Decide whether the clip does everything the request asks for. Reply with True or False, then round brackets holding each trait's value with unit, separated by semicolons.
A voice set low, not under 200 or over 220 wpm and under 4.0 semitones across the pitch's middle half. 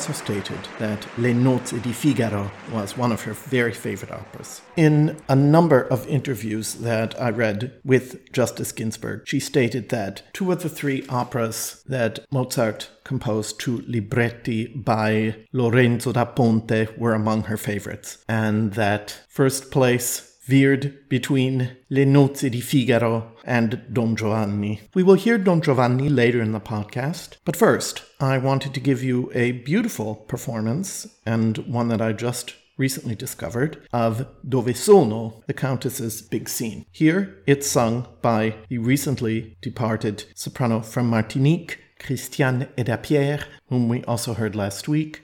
False (120 Hz; 145 wpm; 3.5 semitones)